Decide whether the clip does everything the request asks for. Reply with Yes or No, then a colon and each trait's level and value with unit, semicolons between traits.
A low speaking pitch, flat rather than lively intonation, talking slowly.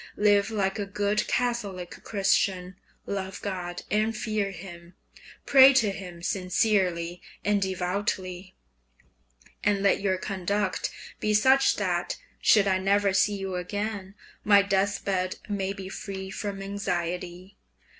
No: high, 195 Hz; narrow, 1.8 semitones; slow, 125 wpm